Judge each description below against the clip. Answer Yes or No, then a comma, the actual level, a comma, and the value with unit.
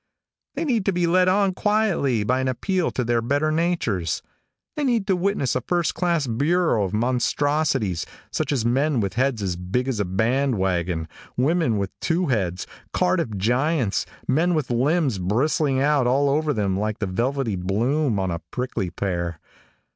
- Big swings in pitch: Yes, wide, 7.6 semitones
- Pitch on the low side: Yes, low, 130 Hz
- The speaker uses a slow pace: No, average, 170 wpm